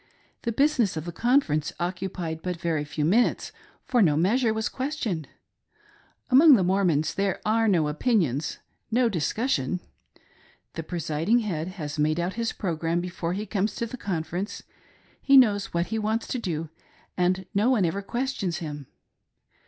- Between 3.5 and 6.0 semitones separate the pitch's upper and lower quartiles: Yes, wide, 5.6 semitones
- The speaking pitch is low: No, medium, 185 Hz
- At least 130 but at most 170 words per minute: Yes, average, 155 wpm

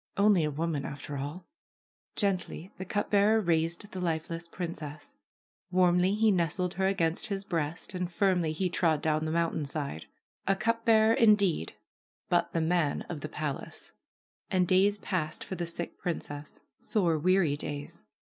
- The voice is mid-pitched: Yes, medium, 175 Hz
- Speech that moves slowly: No, average, 160 wpm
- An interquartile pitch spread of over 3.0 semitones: Yes, average, 3.6 semitones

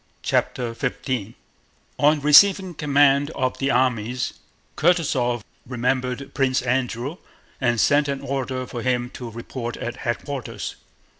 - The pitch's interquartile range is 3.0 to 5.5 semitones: No, narrow, 2.6 semitones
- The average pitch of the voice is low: Yes, low, 130 Hz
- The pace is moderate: No, slow, 120 wpm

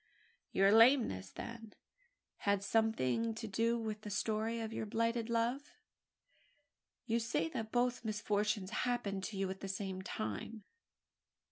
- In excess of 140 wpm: No, slow, 135 wpm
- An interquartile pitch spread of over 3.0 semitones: No, narrow, 2.5 semitones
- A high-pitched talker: Yes, high, 220 Hz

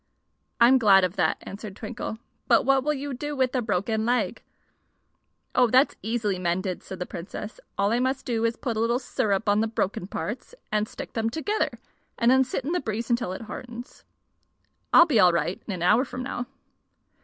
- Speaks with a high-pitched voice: Yes, high, 230 Hz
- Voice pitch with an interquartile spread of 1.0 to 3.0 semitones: No, average, 3.8 semitones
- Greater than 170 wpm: Yes, average, 200 wpm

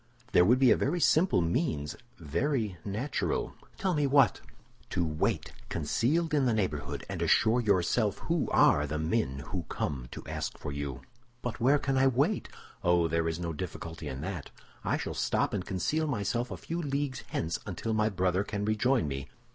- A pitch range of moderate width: No, wide, 8.4 semitones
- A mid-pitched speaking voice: No, low, 105 Hz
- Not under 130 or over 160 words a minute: No, average, 180 wpm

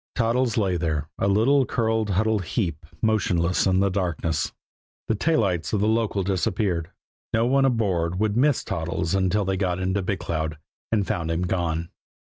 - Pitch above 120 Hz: No, very low, 95 Hz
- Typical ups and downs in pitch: Yes, average, 4.5 semitones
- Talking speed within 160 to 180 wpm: Yes, average, 170 wpm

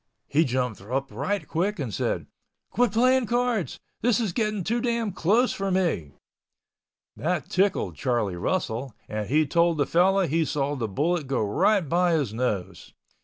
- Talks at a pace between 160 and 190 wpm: Yes, average, 165 wpm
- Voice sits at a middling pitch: Yes, medium, 170 Hz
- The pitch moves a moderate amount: No, wide, 7.7 semitones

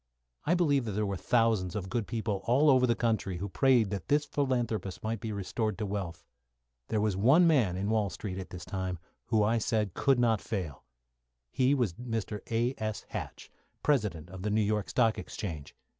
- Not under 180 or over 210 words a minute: Yes, average, 190 wpm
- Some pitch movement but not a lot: Yes, average, 3.8 semitones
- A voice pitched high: No, low, 110 Hz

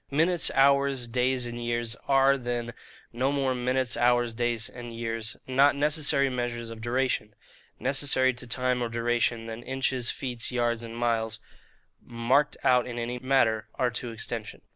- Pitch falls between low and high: No, low, 120 Hz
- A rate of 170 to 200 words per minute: No, average, 155 wpm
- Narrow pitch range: Yes, narrow, 2.0 semitones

